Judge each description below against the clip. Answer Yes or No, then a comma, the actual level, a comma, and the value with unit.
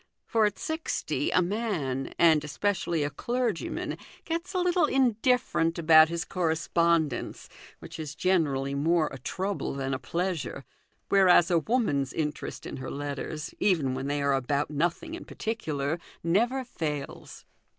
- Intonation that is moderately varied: No, wide, 6.2 semitones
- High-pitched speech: No, medium, 165 Hz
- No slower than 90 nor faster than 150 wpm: Yes, average, 140 wpm